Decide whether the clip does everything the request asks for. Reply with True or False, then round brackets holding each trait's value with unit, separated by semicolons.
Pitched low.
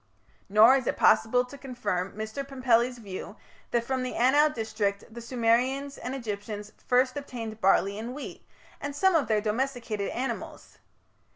False (240 Hz)